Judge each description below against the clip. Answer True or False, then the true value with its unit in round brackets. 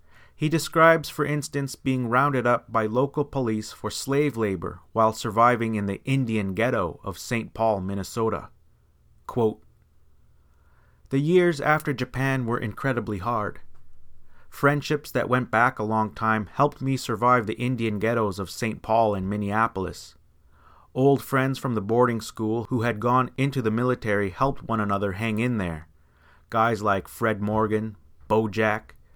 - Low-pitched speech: True (115 Hz)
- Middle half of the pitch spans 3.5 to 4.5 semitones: True (4.1 semitones)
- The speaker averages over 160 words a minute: False (150 wpm)